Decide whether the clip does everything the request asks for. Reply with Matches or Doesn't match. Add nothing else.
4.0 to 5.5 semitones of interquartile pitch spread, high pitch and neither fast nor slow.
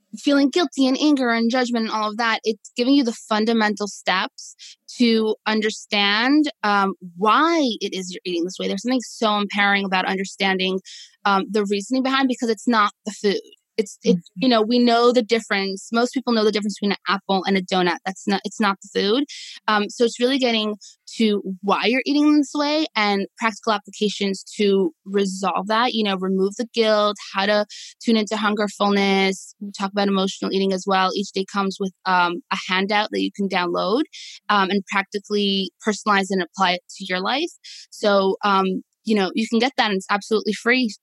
Doesn't match